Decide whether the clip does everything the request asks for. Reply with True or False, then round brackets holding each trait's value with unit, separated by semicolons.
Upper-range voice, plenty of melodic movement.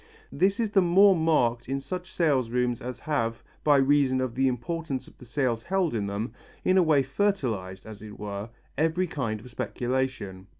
False (130 Hz; 6.0 semitones)